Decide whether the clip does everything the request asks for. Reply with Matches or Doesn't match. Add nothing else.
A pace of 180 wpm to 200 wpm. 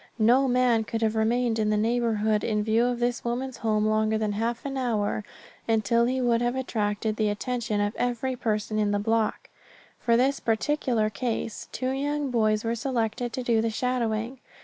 Matches